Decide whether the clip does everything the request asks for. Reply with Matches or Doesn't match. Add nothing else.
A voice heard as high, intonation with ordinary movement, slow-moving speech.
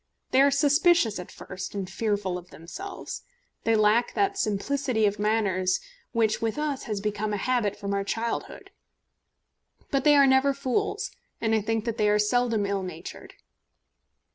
Doesn't match